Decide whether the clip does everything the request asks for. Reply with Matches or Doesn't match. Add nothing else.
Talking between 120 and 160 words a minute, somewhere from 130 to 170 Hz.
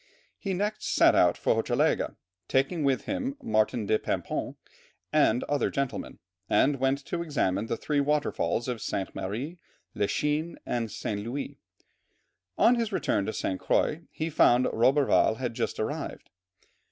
Matches